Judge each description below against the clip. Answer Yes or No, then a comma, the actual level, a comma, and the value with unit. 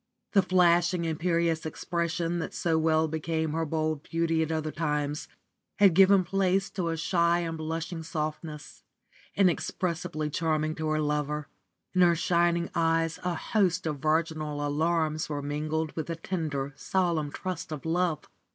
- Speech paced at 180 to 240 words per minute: No, average, 150 wpm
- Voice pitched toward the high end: No, medium, 165 Hz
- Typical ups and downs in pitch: No, narrow, 1.8 semitones